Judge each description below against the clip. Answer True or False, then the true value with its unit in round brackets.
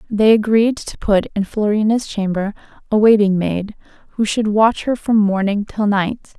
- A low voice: False (210 Hz)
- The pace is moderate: True (170 wpm)